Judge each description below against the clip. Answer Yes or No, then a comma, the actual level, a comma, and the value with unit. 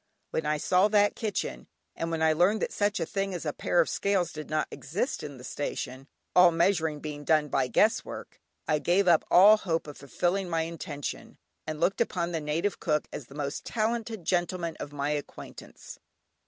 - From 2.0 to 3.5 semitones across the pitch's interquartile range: No, average, 4.2 semitones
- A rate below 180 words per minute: No, average, 195 wpm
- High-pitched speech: No, medium, 165 Hz